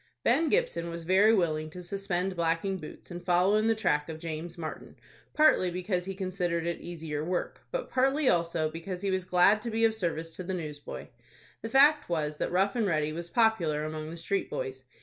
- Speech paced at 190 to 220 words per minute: Yes, fast, 205 wpm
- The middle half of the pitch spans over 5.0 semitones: No, average, 3.6 semitones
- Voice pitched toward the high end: No, medium, 175 Hz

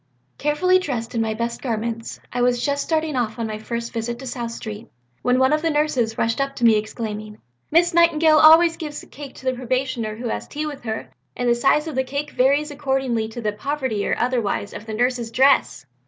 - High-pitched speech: Yes, very high, 250 Hz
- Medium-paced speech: No, fast, 215 wpm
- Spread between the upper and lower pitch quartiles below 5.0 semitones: Yes, average, 4.4 semitones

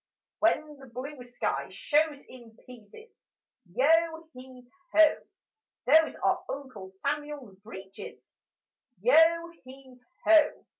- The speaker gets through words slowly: Yes, slow, 100 wpm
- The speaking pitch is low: No, very high, 275 Hz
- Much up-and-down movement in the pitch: No, average, 4.3 semitones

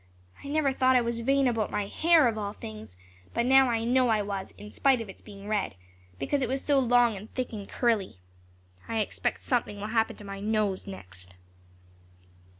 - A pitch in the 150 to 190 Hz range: No, high, 225 Hz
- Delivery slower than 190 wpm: No, average, 200 wpm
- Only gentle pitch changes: No, average, 4.0 semitones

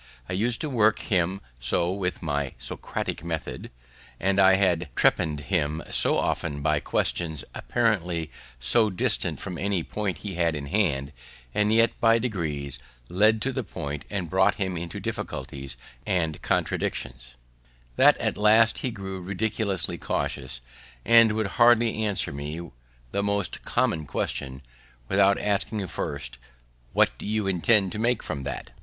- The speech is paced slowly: No, average, 145 wpm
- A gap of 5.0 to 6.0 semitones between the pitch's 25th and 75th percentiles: Yes, wide, 5.5 semitones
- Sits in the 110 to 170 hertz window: No, very low, 95 Hz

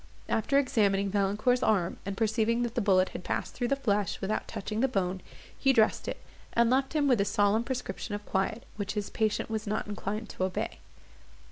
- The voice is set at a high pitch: Yes, high, 215 Hz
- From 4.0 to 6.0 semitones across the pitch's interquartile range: No, average, 3.1 semitones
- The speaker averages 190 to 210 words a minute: Yes, average, 200 wpm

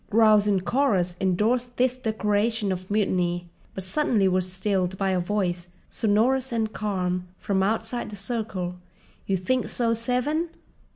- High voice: Yes, high, 205 Hz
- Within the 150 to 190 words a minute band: No, average, 140 wpm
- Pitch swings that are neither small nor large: Yes, average, 3.8 semitones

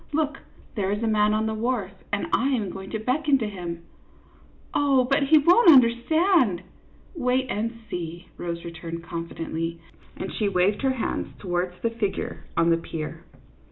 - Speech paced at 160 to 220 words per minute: Yes, average, 180 wpm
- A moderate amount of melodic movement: No, wide, 6.7 semitones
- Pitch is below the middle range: No, high, 210 Hz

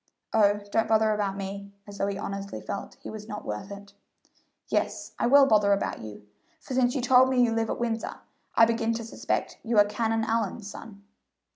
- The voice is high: Yes, high, 215 Hz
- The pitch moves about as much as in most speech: No, narrow, 2.3 semitones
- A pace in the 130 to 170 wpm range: No, average, 200 wpm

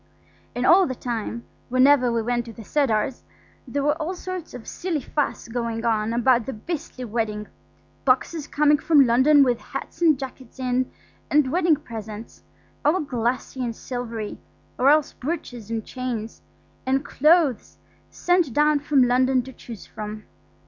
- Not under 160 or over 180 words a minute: No, average, 150 wpm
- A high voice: Yes, very high, 255 Hz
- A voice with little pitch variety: No, average, 4.1 semitones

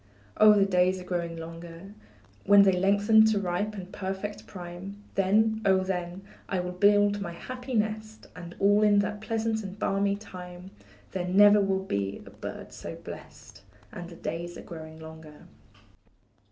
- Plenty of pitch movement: No, average, 2.7 semitones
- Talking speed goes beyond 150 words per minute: Yes, average, 165 wpm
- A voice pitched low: No, high, 195 Hz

